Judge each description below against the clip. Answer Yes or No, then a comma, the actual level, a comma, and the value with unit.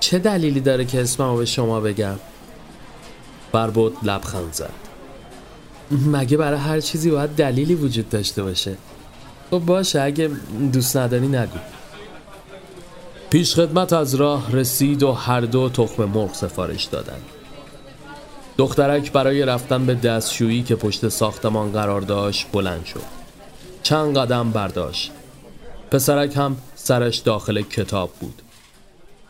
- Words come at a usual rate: Yes, average, 120 wpm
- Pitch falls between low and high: No, low, 130 Hz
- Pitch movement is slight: No, average, 5.1 semitones